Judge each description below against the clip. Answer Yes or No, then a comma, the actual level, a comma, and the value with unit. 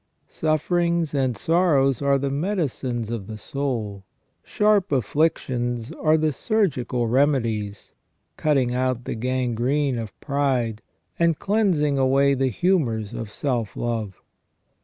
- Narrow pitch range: No, average, 4.6 semitones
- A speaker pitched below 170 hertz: Yes, low, 135 Hz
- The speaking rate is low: Yes, slow, 115 wpm